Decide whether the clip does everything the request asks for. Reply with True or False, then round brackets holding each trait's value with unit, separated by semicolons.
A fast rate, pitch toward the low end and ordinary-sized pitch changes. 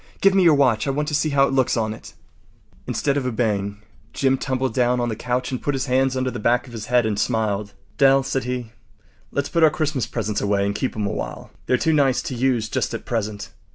True (245 wpm; 125 Hz; 3.7 semitones)